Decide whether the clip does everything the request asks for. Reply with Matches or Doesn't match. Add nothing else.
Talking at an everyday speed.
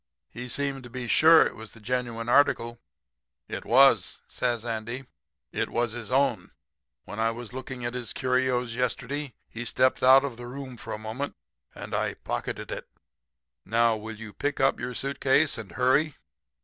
Matches